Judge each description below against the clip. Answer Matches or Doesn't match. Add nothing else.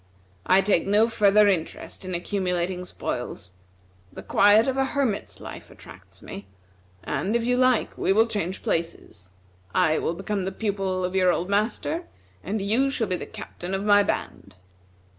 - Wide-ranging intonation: Doesn't match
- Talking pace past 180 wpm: Doesn't match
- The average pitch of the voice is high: Matches